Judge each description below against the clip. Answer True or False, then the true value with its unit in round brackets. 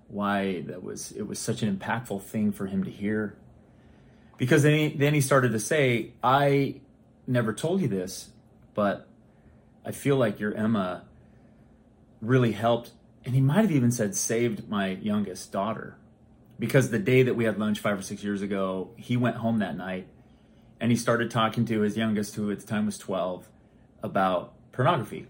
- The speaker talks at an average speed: True (180 wpm)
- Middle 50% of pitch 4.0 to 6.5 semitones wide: False (2.8 semitones)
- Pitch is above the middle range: False (110 Hz)